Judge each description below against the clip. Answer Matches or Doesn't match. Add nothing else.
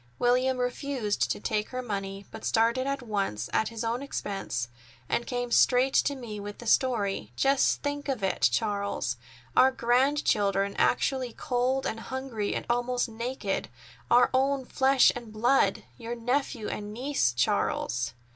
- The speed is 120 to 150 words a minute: Matches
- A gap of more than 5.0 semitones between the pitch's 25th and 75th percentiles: Doesn't match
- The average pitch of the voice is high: Matches